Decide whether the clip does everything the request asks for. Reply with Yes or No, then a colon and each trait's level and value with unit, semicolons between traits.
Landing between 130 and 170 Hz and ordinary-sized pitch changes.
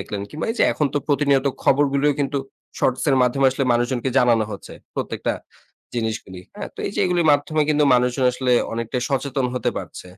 Yes: low, 135 Hz; average, 3.0 semitones